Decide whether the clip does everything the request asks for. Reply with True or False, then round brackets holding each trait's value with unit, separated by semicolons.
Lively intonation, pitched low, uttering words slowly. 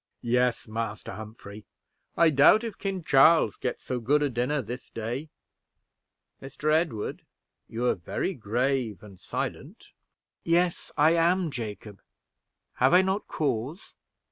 True (6.1 semitones; 130 Hz; 130 wpm)